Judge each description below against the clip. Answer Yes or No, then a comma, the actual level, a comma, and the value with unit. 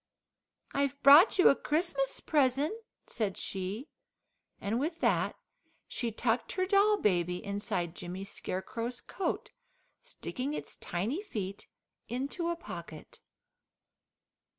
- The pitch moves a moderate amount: No, wide, 7.8 semitones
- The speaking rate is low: Yes, slow, 110 wpm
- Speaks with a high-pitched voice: Yes, high, 245 Hz